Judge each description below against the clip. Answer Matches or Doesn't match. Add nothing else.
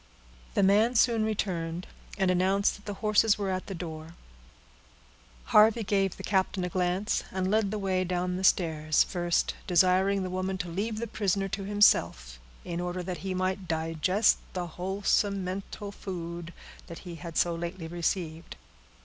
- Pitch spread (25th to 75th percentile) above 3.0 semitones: Doesn't match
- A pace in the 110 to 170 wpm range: Matches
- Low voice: Doesn't match